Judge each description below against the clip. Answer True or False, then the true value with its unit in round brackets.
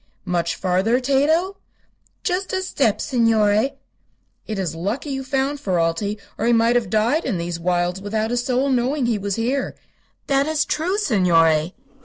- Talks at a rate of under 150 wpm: False (160 wpm)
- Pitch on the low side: False (230 Hz)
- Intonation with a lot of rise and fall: True (6.6 semitones)